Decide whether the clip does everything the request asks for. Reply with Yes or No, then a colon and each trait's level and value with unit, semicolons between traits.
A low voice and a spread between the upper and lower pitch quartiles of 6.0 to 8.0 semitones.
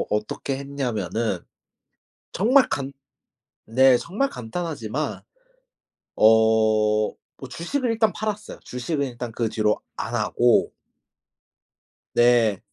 Yes: low, 125 Hz; wide, 6.9 semitones